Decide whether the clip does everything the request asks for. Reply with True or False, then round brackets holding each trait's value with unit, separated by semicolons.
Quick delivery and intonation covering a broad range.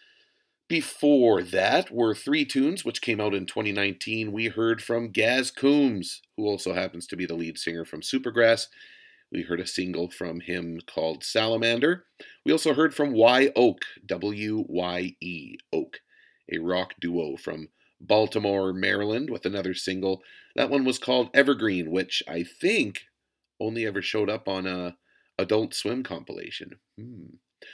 False (145 wpm; 7.2 semitones)